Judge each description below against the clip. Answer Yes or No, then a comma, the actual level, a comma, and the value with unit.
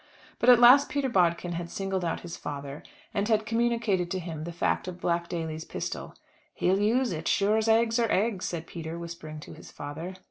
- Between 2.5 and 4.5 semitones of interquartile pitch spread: No, average, 4.9 semitones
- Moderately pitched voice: Yes, medium, 180 Hz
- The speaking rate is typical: No, fast, 210 wpm